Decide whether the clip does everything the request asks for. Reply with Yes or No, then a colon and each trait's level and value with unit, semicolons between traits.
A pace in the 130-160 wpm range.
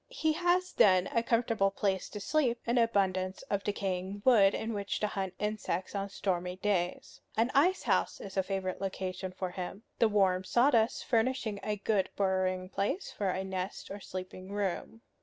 No: average, 175 wpm